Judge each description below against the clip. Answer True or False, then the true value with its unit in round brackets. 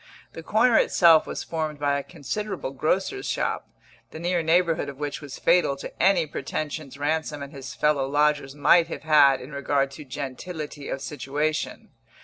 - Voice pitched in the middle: True (150 Hz)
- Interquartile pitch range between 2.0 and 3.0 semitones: True (2.7 semitones)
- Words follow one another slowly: False (165 wpm)